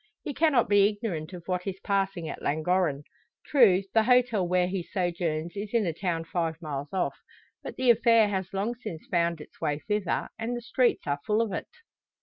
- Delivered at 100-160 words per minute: No, average, 195 wpm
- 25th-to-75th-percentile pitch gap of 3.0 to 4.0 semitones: No, average, 4.6 semitones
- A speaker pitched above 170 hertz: Yes, high, 190 Hz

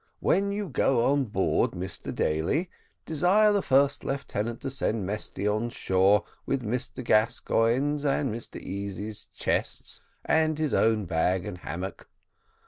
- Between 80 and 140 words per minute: Yes, slow, 135 wpm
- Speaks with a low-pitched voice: Yes, low, 115 Hz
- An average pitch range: No, wide, 6.0 semitones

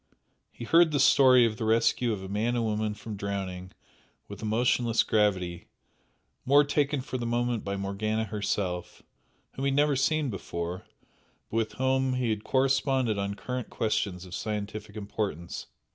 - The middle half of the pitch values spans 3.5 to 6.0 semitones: Yes, average, 4.3 semitones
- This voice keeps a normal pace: Yes, average, 160 wpm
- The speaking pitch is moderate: No, low, 110 Hz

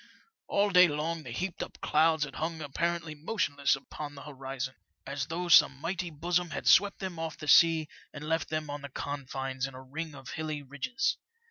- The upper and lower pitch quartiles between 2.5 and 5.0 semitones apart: Yes, average, 3.0 semitones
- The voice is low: No, medium, 155 Hz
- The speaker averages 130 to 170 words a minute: No, average, 195 wpm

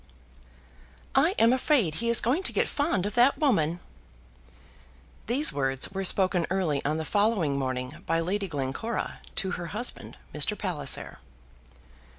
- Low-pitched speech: No, high, 190 Hz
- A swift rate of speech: No, average, 145 wpm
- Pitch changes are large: Yes, wide, 7.3 semitones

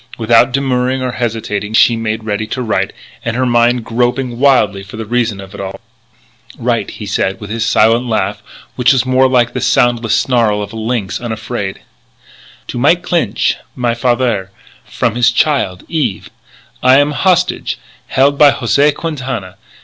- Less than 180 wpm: Yes, average, 160 wpm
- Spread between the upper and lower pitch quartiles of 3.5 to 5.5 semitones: No, average, 2.9 semitones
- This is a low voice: Yes, low, 120 Hz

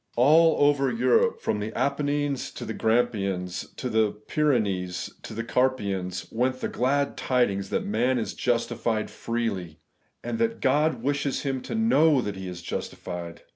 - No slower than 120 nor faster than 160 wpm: Yes, average, 155 wpm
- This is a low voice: Yes, low, 120 Hz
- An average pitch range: No, wide, 5.7 semitones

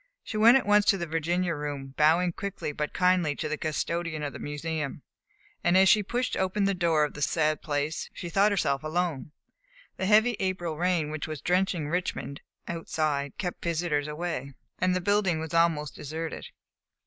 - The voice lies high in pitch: No, medium, 165 Hz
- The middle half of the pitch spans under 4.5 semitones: Yes, average, 3.4 semitones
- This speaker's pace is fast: No, average, 180 wpm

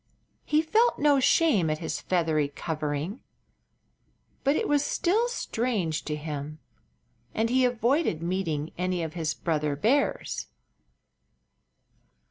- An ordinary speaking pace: No, slow, 115 wpm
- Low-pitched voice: No, medium, 180 Hz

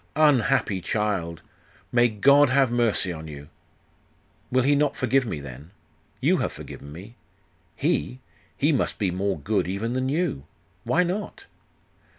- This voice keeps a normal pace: Yes, average, 145 wpm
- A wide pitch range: Yes, wide, 7.6 semitones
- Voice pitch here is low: Yes, low, 110 Hz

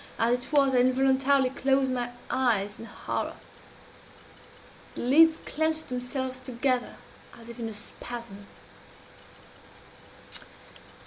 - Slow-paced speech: Yes, slow, 110 wpm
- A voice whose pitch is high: Yes, very high, 255 Hz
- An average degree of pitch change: No, narrow, 2.1 semitones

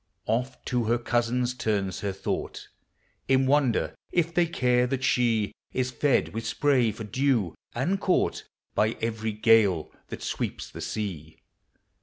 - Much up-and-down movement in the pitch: No, average, 3.3 semitones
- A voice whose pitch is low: Yes, low, 120 Hz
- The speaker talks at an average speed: Yes, average, 145 wpm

